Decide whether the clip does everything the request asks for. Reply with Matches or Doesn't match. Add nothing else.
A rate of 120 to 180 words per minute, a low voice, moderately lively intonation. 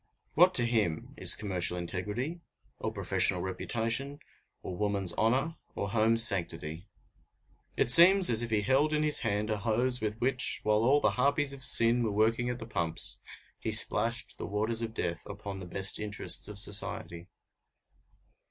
Matches